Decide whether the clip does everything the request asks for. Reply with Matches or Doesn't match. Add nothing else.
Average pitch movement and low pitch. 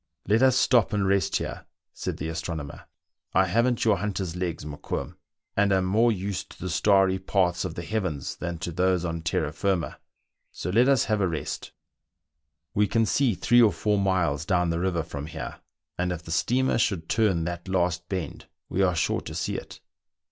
Matches